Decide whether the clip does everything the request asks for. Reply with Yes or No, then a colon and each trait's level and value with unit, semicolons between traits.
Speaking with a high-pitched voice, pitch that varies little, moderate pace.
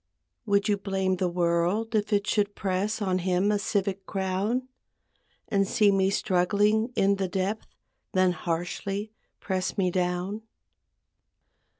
No: high, 195 Hz; narrow, 2.0 semitones; slow, 130 wpm